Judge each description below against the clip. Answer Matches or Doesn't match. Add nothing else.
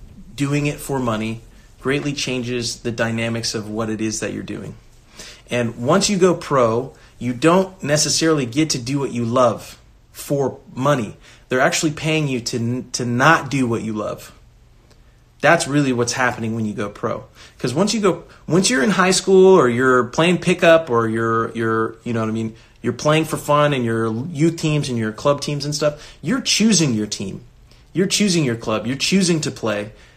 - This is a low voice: Matches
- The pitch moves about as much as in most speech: Doesn't match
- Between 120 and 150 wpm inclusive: Doesn't match